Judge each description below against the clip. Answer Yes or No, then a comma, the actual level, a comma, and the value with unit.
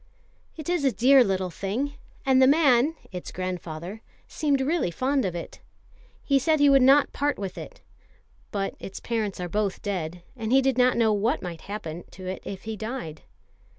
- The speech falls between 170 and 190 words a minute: Yes, average, 185 wpm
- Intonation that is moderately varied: No, wide, 6.5 semitones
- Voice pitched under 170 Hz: No, high, 225 Hz